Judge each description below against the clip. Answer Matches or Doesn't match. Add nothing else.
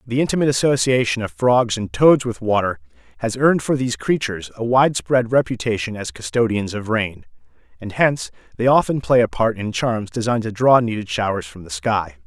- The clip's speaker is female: Doesn't match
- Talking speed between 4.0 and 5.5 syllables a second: Doesn't match